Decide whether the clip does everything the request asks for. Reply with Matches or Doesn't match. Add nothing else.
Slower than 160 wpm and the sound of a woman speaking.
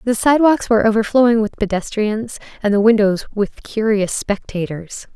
Matches